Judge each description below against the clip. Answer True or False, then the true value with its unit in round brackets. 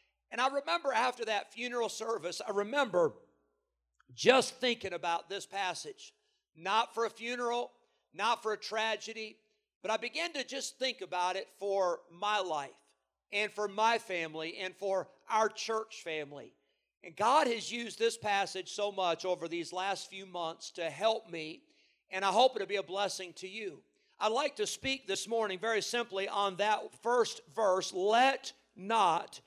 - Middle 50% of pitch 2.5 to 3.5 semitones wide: False (4.0 semitones)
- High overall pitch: True (210 Hz)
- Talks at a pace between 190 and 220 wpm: False (165 wpm)